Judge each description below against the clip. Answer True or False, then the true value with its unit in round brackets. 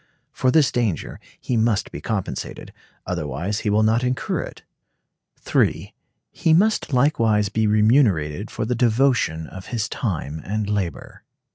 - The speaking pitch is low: True (110 Hz)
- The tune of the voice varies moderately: True (4.0 semitones)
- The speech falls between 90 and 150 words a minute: True (140 wpm)